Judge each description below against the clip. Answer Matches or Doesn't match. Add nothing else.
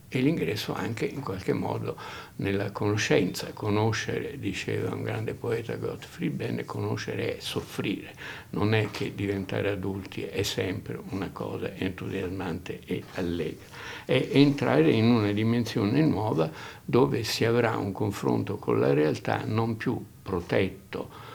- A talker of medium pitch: Doesn't match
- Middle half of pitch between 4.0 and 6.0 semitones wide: Matches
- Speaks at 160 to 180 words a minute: Doesn't match